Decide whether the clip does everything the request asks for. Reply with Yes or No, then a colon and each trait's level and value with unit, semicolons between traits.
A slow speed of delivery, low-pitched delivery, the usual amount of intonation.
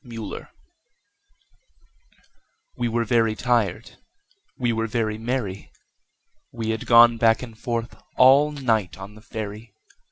No: slow, 120 wpm; low, 115 Hz; narrow, 1.7 semitones